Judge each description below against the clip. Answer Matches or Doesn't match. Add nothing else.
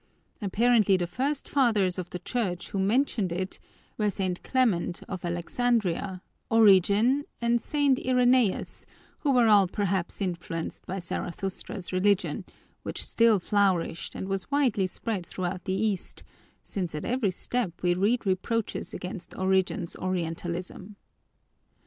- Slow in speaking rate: Matches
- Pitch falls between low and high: Doesn't match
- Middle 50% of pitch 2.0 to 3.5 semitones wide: Doesn't match